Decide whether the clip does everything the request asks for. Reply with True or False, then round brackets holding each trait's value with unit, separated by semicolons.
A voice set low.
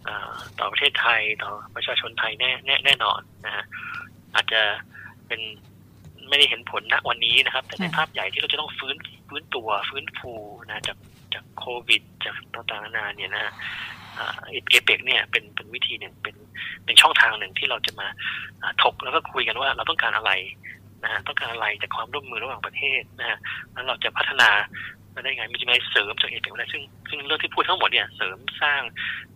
True (115 Hz)